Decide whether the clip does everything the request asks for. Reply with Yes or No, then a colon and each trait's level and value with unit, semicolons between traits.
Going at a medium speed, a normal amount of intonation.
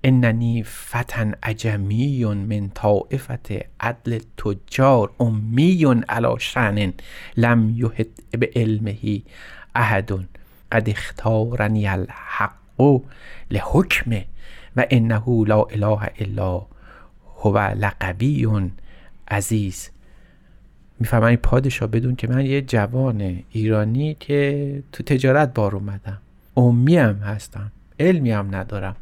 No: slow, 95 wpm; average, 3.4 semitones